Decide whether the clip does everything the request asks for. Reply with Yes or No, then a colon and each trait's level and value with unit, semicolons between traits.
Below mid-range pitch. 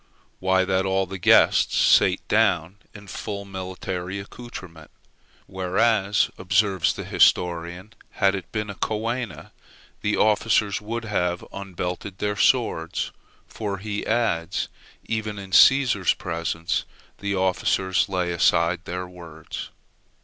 Yes: very low, 95 Hz